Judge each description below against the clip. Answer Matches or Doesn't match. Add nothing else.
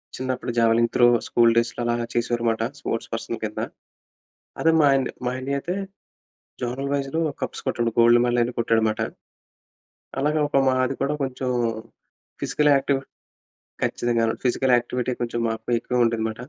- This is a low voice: Matches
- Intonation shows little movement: Matches